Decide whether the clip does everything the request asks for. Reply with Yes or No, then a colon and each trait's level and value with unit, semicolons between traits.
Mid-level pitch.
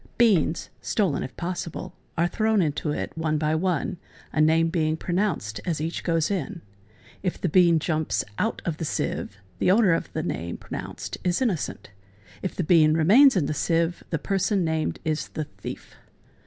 Yes: medium, 165 Hz